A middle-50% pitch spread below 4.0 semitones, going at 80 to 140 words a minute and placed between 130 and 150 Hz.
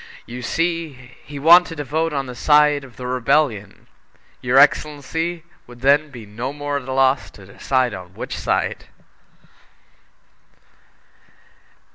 Yes: average, 3.3 semitones; slow, 135 wpm; medium, 140 Hz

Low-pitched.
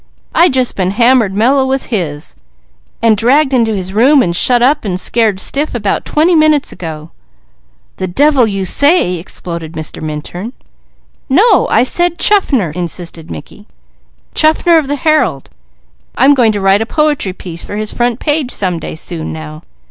No: high, 225 Hz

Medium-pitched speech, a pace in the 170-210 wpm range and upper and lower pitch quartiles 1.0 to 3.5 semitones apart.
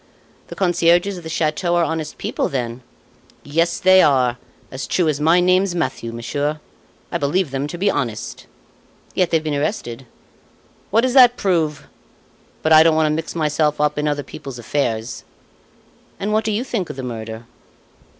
No: medium, 155 Hz; average, 175 wpm; average, 4.3 semitones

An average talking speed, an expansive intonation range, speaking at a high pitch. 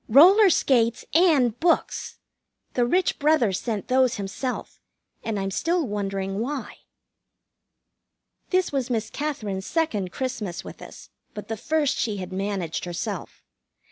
No: slow, 130 wpm; wide, 6.8 semitones; high, 235 Hz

